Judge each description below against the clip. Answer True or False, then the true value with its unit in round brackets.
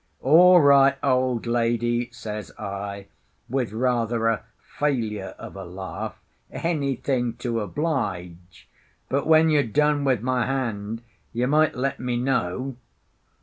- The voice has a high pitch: False (125 Hz)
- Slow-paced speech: True (125 wpm)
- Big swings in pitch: False (4.1 semitones)